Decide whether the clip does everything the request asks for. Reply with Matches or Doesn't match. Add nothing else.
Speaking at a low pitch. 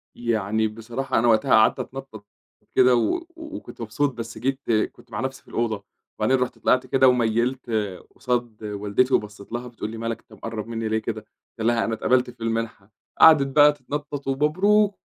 Matches